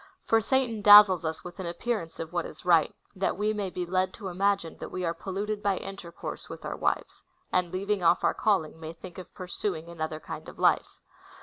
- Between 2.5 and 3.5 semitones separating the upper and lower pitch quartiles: Yes, average, 3.1 semitones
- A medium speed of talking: No, fast, 215 wpm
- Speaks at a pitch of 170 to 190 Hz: Yes, medium, 185 Hz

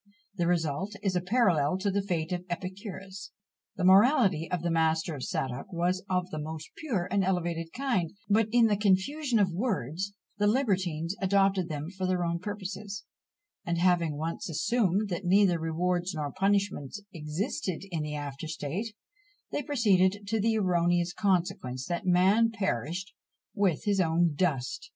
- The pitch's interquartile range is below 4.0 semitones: Yes, average, 3.5 semitones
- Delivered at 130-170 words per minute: Yes, average, 160 wpm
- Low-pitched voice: No, medium, 180 Hz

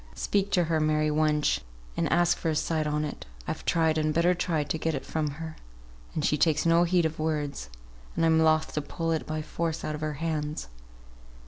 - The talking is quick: Yes, fast, 215 wpm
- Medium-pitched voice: Yes, medium, 155 Hz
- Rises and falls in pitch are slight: Yes, narrow, 1.3 semitones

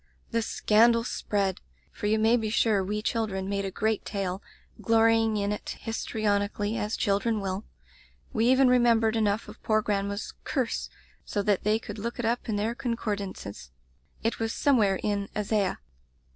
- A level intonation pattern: Yes, narrow, 2.1 semitones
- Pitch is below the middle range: No, high, 215 Hz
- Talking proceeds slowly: No, average, 170 wpm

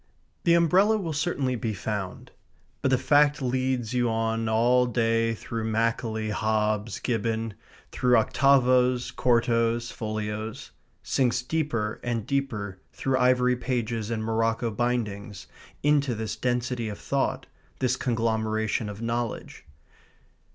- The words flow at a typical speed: No, slow, 120 wpm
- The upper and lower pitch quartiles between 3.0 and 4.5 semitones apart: No, narrow, 2.4 semitones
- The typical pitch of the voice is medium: No, low, 115 Hz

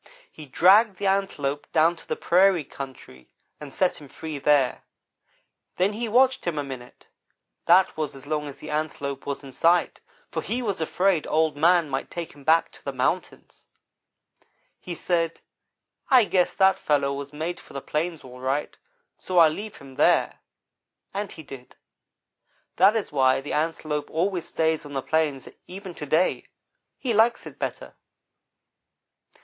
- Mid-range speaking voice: Yes, medium, 160 Hz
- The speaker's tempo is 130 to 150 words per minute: No, average, 165 wpm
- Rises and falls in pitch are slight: No, average, 4.6 semitones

